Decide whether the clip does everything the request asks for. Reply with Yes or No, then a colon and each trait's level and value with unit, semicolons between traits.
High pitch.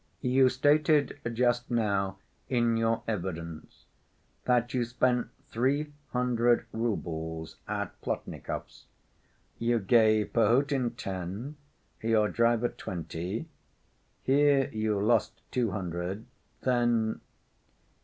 No: low, 115 Hz